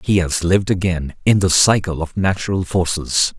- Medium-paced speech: Yes, average, 175 wpm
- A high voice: No, very low, 90 Hz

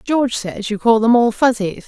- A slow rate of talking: No, fast, 225 wpm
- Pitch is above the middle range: Yes, high, 230 Hz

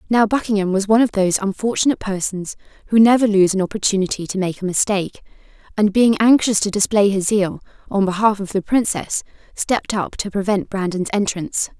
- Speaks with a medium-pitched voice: No, high, 200 Hz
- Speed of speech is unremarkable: Yes, average, 180 wpm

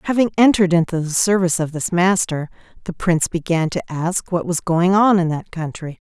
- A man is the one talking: No, female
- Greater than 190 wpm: Yes, average, 200 wpm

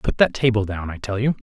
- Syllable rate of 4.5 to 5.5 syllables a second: No, 5.9 syllables/s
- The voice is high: No, low, 110 Hz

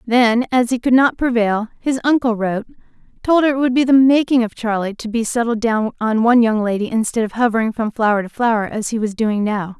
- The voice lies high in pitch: Yes, high, 230 Hz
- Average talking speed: No, fast, 235 wpm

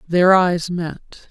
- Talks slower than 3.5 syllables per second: Yes, 2.6 syllables/s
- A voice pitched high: No, medium, 175 Hz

